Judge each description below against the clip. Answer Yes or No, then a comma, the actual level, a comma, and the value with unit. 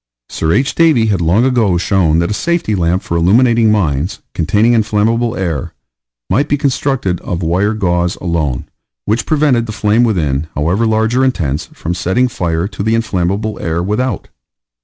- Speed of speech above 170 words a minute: No, average, 165 wpm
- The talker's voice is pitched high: No, low, 105 Hz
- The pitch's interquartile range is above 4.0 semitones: Yes, average, 5.3 semitones